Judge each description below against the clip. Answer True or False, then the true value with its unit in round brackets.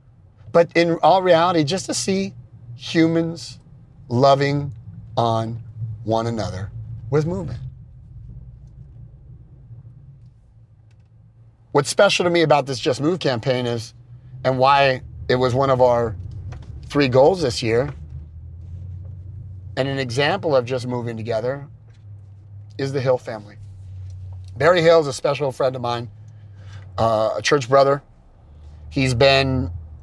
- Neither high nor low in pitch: False (120 Hz)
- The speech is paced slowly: True (120 wpm)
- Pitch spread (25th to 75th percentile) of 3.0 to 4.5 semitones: True (3.9 semitones)